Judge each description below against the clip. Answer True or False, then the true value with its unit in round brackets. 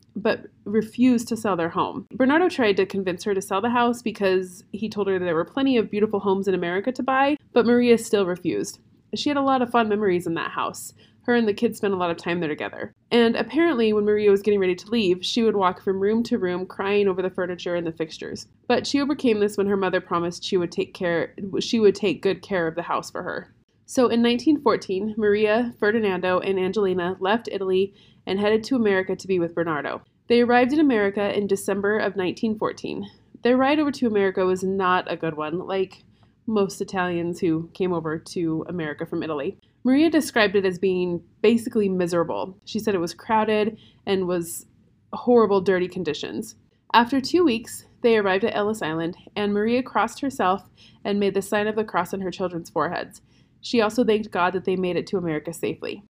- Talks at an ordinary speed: False (210 wpm)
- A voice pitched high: True (200 Hz)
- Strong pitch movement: False (3.9 semitones)